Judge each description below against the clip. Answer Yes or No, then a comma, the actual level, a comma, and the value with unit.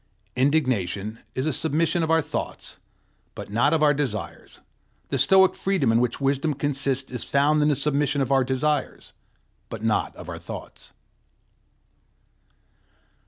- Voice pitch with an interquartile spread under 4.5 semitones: Yes, average, 2.9 semitones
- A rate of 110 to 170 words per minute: Yes, average, 145 wpm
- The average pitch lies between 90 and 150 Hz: Yes, medium, 140 Hz